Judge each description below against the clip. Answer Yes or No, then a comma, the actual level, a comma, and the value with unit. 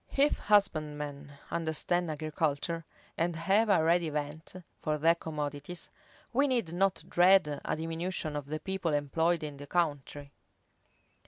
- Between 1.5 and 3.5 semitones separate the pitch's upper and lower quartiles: Yes, average, 3.0 semitones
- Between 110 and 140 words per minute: Yes, slow, 135 wpm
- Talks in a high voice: No, medium, 160 Hz